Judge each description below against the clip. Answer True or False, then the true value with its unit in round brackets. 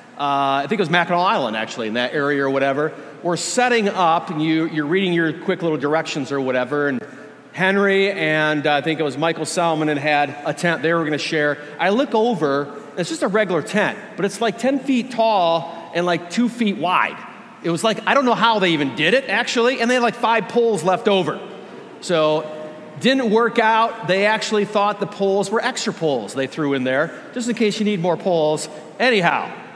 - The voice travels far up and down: True (6.2 semitones)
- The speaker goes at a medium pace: False (215 wpm)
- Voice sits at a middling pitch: True (175 Hz)